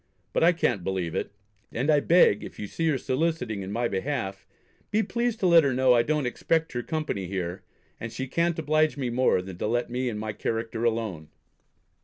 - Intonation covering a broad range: Yes, wide, 6.7 semitones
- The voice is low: Yes, low, 125 Hz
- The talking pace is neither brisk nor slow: No, fast, 210 wpm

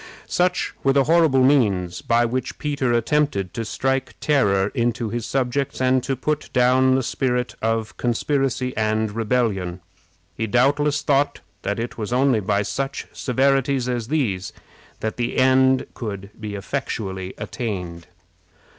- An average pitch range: Yes, average, 3.9 semitones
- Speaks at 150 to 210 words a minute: No, average, 140 wpm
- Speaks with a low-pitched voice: Yes, low, 125 Hz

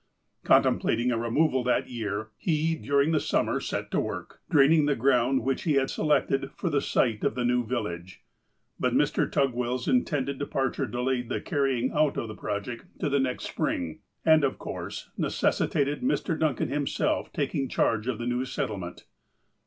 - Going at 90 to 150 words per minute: No, average, 175 wpm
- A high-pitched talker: No, low, 130 Hz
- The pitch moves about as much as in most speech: Yes, average, 3.3 semitones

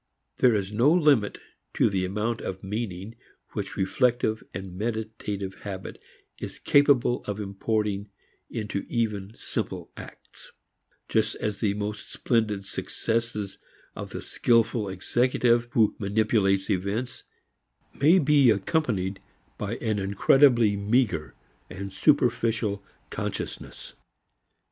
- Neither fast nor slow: No, slow, 110 wpm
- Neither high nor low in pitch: No, low, 105 Hz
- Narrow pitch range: No, average, 3.2 semitones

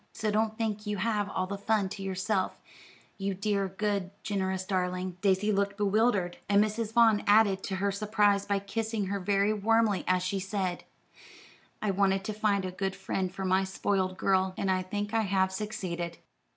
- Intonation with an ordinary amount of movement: No, narrow, 1.9 semitones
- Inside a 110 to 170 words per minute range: No, average, 180 wpm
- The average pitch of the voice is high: Yes, high, 200 Hz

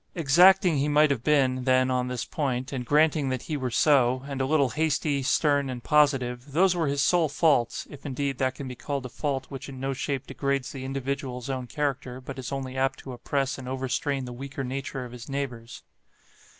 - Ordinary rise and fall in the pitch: No, narrow, 2.0 semitones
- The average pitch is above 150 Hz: No, low, 135 Hz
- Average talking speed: No, fast, 210 wpm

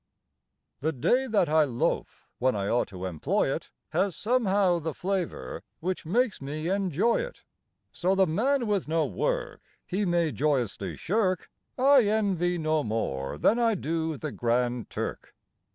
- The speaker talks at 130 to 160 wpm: Yes, average, 150 wpm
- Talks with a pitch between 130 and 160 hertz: No, medium, 175 Hz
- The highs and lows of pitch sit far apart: Yes, wide, 6.8 semitones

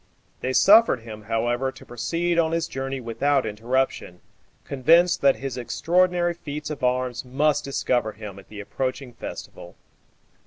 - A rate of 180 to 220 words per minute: No, average, 145 wpm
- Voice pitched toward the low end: Yes, low, 130 Hz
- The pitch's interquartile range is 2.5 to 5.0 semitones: Yes, average, 4.4 semitones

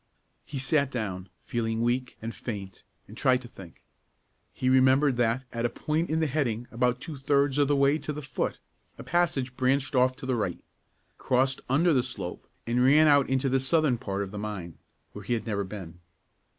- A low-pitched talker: Yes, low, 130 Hz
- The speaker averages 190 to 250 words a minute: Yes, average, 200 wpm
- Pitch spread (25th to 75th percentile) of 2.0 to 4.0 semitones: Yes, average, 3.7 semitones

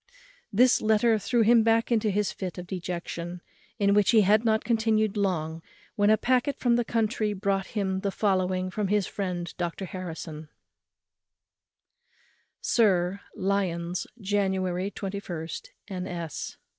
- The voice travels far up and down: No, average, 3.0 semitones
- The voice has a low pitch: No, high, 200 Hz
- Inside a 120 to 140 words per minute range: Yes, slow, 135 wpm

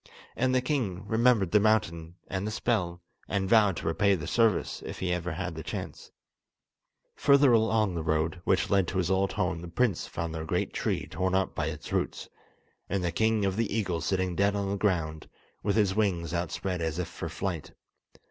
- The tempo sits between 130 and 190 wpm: No, average, 200 wpm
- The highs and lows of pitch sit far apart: No, average, 3.8 semitones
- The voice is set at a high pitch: No, very low, 95 Hz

